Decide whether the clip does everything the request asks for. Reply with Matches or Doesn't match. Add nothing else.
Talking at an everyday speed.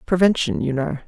Matches